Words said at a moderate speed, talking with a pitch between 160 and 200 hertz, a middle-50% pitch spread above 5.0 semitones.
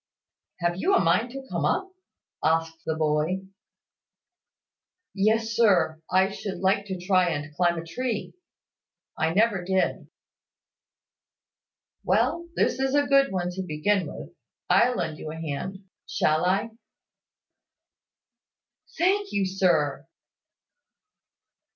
No: slow, 120 wpm; high, 190 Hz; wide, 5.5 semitones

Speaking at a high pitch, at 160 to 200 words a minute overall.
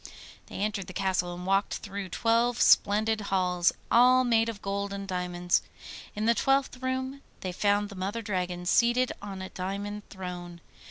Yes: high, 200 Hz; average, 165 wpm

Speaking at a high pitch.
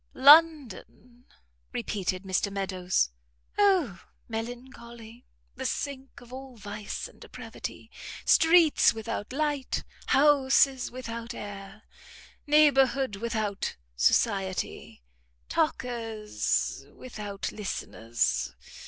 Yes: high, 235 Hz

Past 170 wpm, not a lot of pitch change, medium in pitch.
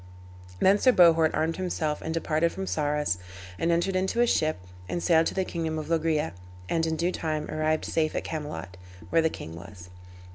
Yes: average, 190 wpm; narrow, 1.6 semitones; medium, 160 Hz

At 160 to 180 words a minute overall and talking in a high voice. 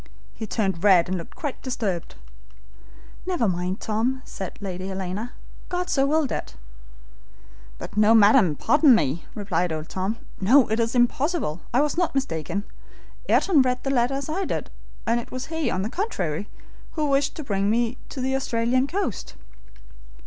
Yes: average, 165 wpm; high, 230 Hz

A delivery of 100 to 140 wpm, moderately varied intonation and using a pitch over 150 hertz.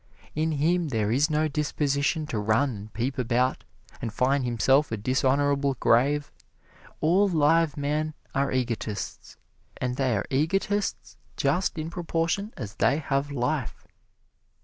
No: slow, 135 wpm; average, 3.9 semitones; medium, 140 Hz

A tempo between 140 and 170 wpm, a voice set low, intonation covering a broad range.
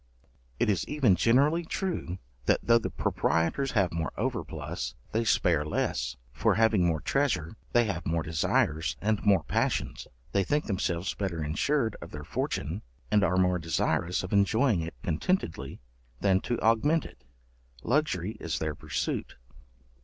Yes: average, 150 wpm; very low, 95 Hz; wide, 5.8 semitones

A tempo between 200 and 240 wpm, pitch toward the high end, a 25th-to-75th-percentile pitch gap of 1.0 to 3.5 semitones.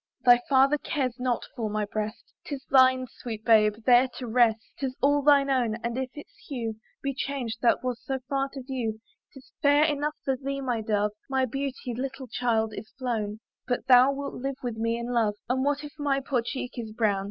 Yes: fast, 205 wpm; very high, 255 Hz; average, 3.1 semitones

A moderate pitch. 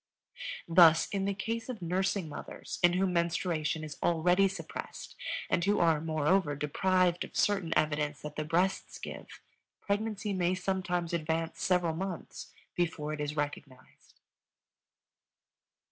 Yes: medium, 175 Hz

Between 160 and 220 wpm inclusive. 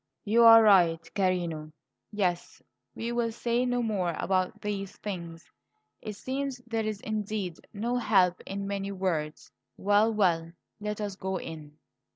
No: average, 145 wpm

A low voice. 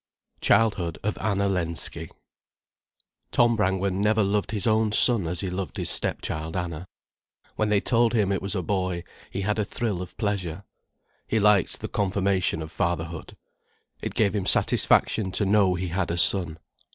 Yes: very low, 95 Hz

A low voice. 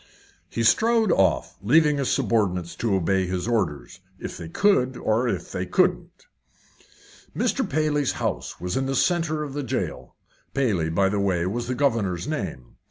Yes: low, 115 Hz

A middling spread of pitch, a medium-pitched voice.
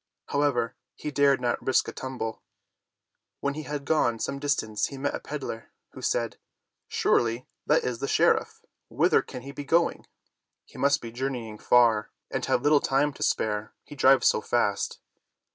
No: average, 3.5 semitones; low, 130 Hz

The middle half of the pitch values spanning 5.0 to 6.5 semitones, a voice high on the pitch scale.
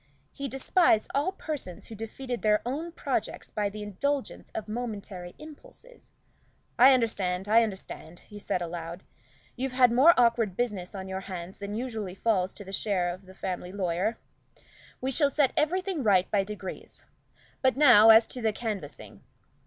Yes: average, 5.3 semitones; high, 215 Hz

